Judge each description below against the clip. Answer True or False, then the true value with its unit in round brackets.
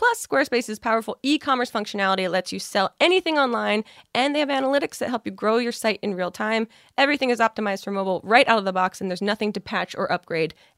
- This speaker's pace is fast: True (235 wpm)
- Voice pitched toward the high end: True (220 Hz)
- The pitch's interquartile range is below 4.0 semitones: False (5.1 semitones)